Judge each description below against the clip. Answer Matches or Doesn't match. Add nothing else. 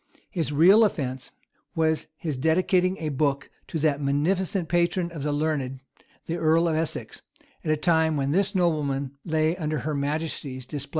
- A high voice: Doesn't match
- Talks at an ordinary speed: Matches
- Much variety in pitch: Doesn't match